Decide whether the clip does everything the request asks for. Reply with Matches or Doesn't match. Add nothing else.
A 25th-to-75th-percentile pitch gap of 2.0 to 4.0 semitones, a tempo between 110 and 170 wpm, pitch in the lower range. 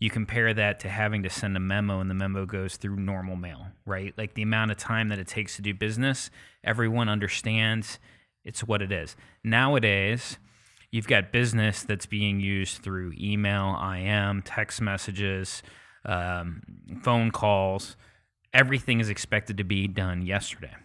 Matches